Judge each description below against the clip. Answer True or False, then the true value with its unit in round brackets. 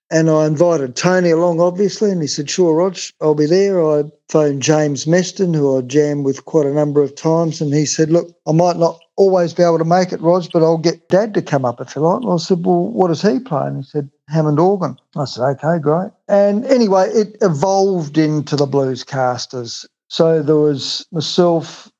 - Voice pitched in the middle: True (165 Hz)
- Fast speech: True (220 wpm)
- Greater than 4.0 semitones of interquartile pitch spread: False (3.5 semitones)